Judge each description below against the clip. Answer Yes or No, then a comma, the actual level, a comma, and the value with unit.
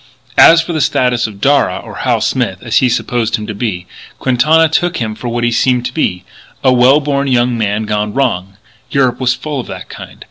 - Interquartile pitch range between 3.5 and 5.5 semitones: Yes, average, 4.1 semitones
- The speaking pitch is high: No, low, 125 Hz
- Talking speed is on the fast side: Yes, fast, 215 wpm